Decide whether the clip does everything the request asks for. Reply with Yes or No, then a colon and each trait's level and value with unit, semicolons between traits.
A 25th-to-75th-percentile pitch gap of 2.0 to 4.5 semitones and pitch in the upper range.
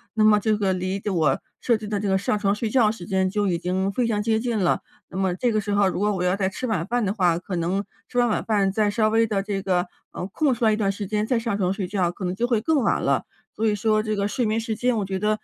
Yes: narrow, 2.5 semitones; high, 205 Hz